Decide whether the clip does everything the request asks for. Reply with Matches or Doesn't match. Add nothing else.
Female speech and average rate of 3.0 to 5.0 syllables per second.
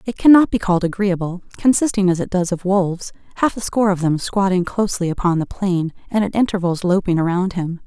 Doesn't match